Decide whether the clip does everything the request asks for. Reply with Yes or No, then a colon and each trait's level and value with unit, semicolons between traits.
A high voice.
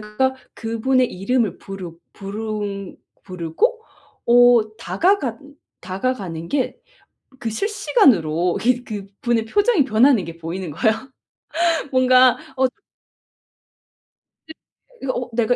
Yes: high, 225 Hz